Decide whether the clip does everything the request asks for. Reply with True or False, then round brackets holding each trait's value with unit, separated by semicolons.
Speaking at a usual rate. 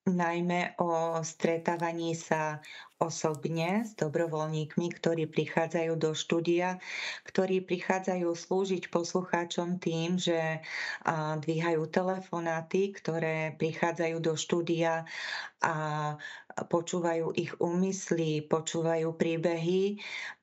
False (85 wpm)